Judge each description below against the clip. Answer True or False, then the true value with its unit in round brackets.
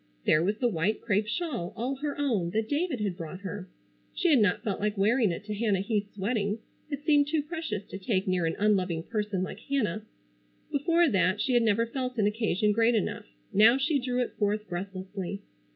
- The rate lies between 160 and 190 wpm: False (200 wpm)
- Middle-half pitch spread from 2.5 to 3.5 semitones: False (4.4 semitones)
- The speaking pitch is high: True (210 Hz)